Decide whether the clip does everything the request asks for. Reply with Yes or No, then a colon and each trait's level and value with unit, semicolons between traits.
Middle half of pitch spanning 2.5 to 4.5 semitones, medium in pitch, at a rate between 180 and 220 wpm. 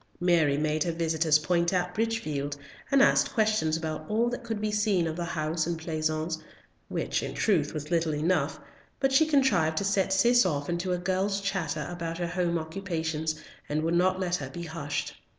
Yes: average, 3.7 semitones; medium, 170 Hz; average, 190 wpm